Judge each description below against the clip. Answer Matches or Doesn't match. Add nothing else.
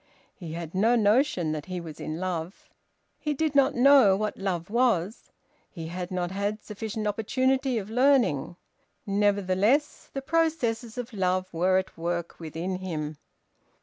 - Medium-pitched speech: Doesn't match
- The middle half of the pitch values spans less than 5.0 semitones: Doesn't match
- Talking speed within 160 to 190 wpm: Doesn't match